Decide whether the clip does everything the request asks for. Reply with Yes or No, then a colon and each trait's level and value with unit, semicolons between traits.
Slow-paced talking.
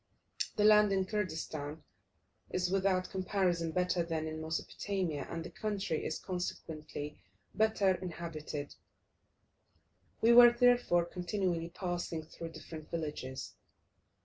Yes: slow, 110 wpm